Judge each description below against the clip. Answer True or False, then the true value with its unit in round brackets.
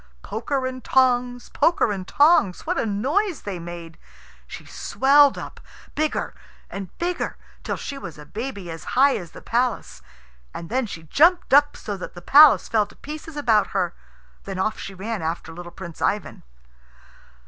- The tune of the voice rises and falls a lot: True (7.3 semitones)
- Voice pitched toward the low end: False (225 Hz)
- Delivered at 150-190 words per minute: True (170 wpm)